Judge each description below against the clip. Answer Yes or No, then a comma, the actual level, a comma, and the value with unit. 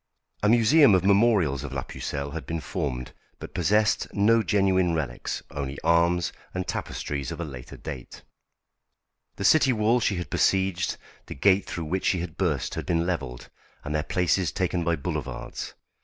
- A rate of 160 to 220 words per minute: Yes, average, 170 wpm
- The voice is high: No, very low, 85 Hz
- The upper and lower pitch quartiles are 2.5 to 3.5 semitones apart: No, average, 5.3 semitones